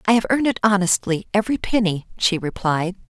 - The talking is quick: No, average, 170 wpm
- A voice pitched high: Yes, high, 195 Hz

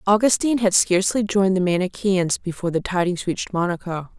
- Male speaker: No, female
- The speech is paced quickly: No, average, 160 wpm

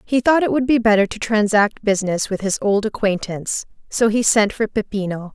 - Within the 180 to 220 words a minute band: Yes, average, 200 wpm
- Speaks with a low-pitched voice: No, high, 215 Hz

